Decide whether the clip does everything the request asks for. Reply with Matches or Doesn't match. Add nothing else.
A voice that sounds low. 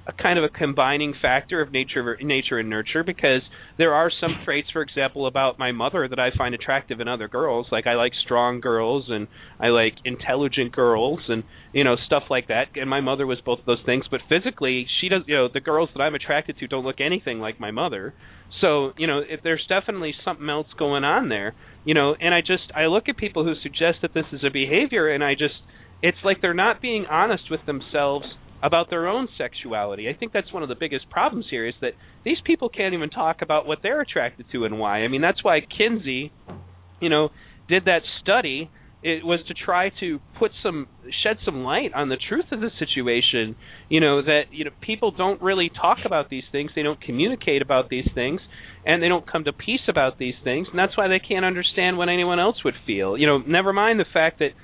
Doesn't match